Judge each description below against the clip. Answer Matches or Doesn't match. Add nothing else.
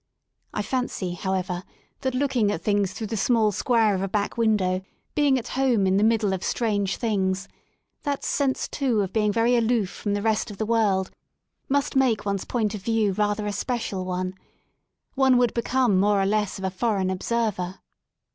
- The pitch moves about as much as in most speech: Matches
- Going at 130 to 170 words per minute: Doesn't match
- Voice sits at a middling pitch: Doesn't match